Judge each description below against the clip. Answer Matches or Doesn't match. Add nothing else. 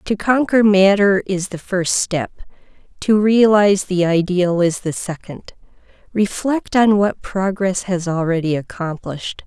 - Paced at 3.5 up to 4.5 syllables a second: Matches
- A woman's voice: Matches